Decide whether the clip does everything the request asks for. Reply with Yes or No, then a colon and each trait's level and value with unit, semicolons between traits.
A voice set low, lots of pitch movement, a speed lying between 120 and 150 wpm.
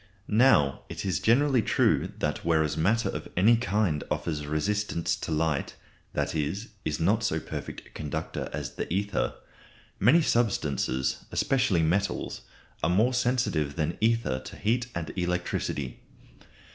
Yes: very low, 90 Hz; wide, 6.5 semitones; average, 140 wpm